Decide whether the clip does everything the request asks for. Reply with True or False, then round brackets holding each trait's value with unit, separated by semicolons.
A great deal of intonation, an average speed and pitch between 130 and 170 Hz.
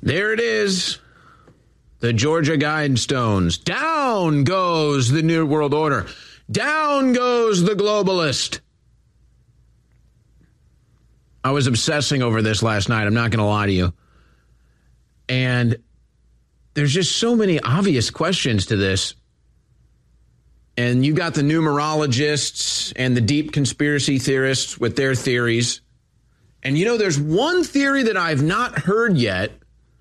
False (6.7 semitones; 125 wpm; 135 Hz)